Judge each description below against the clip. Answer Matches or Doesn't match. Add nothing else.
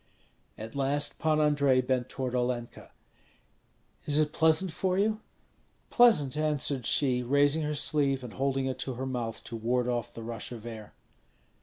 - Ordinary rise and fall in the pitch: Matches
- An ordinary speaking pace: Matches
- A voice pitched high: Doesn't match